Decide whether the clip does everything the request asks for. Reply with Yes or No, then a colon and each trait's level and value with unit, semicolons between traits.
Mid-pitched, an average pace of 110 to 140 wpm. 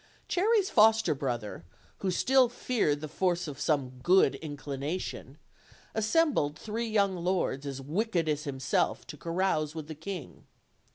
Yes: medium, 165 Hz; slow, 135 wpm